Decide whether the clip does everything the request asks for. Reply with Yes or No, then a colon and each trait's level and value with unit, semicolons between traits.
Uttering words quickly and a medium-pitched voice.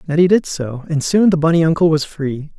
Yes: fast, 230 wpm; medium, 160 Hz